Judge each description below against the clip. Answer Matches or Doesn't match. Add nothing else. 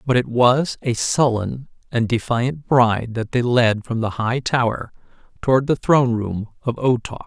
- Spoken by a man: Matches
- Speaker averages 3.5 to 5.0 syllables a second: Matches